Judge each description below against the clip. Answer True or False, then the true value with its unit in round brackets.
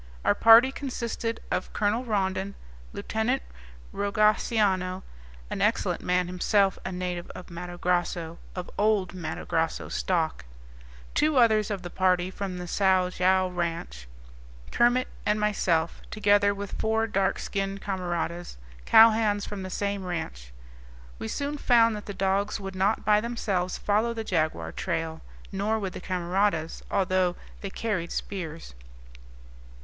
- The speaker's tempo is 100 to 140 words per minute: True (135 wpm)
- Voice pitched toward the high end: True (195 Hz)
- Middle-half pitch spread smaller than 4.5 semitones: True (3.0 semitones)